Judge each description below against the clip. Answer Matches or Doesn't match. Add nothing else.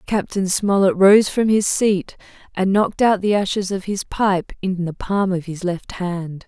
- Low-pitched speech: Doesn't match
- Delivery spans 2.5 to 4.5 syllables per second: Matches